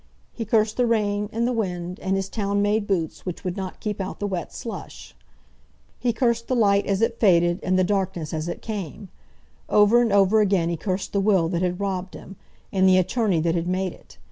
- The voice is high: Yes, high, 195 Hz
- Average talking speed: No, fast, 220 wpm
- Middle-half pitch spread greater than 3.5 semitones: No, average, 2.8 semitones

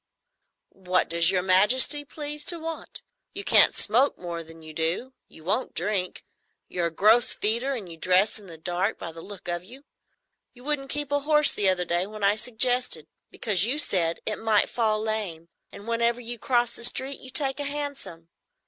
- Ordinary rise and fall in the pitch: No, wide, 6.4 semitones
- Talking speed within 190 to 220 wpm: Yes, average, 195 wpm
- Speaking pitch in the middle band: No, high, 215 Hz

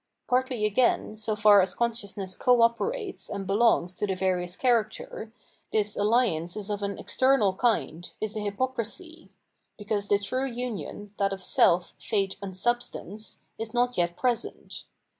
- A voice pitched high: Yes, high, 210 Hz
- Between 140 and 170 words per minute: Yes, average, 160 wpm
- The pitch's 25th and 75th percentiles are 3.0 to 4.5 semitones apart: Yes, average, 3.5 semitones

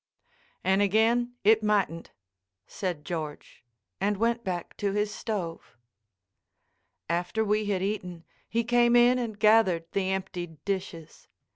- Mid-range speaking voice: No, high, 200 Hz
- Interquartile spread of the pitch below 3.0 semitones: No, average, 3.8 semitones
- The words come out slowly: Yes, slow, 125 wpm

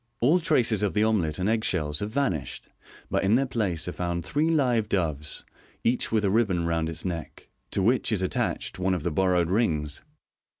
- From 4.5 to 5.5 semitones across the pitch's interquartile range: Yes, average, 5.2 semitones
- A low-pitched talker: Yes, very low, 95 Hz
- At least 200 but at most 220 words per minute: Yes, fast, 205 wpm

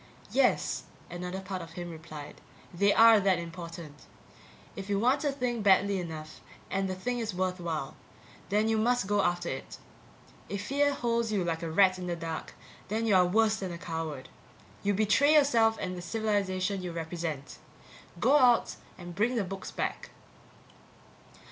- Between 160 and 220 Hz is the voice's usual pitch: Yes, high, 190 Hz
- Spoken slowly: No, average, 165 wpm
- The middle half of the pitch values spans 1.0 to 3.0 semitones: No, average, 4.3 semitones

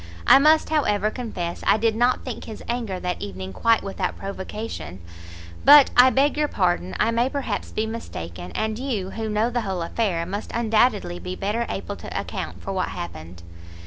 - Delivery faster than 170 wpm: Yes, average, 180 wpm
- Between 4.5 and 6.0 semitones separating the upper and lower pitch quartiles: Yes, average, 4.8 semitones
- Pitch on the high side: Yes, high, 215 Hz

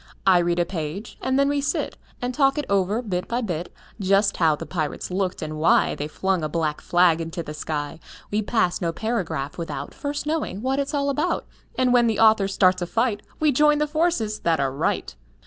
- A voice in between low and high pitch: No, high, 195 Hz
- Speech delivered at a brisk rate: Yes, fast, 215 wpm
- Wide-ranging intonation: Yes, wide, 7.3 semitones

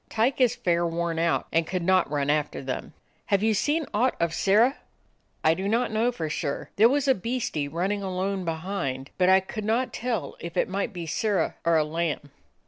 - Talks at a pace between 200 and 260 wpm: Yes, fast, 205 wpm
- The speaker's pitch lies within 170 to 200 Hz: Yes, medium, 185 Hz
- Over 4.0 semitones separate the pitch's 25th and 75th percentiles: Yes, average, 5.1 semitones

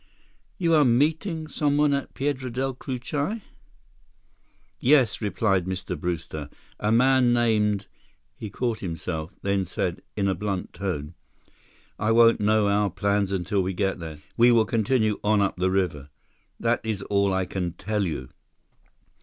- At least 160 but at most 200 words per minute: No, average, 150 wpm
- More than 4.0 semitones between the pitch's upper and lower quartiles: Yes, average, 4.4 semitones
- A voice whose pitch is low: Yes, low, 105 Hz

